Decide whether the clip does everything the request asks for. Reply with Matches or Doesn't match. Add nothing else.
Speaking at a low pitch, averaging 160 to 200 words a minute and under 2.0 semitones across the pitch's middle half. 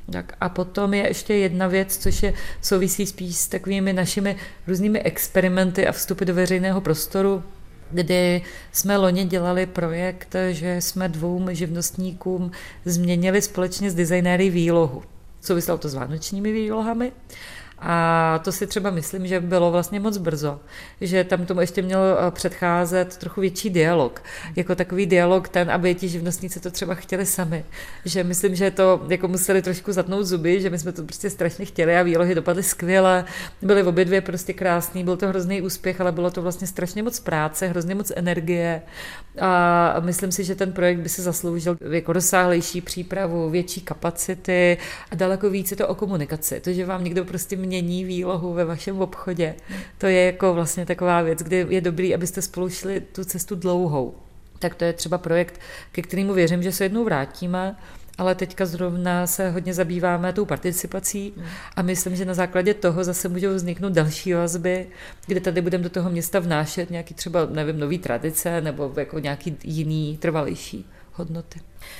Doesn't match